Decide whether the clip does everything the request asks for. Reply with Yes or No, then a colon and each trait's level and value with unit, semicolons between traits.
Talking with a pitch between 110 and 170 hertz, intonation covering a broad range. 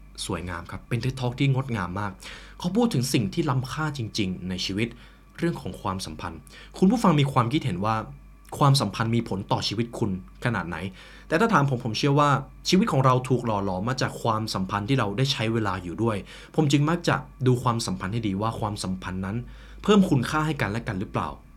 Yes: low, 115 Hz; wide, 6.0 semitones